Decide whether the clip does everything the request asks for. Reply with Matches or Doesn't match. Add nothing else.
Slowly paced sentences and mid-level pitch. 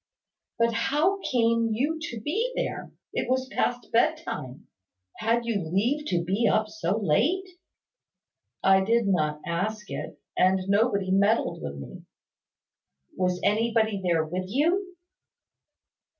Doesn't match